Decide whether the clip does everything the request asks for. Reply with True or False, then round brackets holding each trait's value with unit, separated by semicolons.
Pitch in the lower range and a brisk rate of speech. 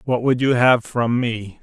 True (120 Hz; 220 wpm)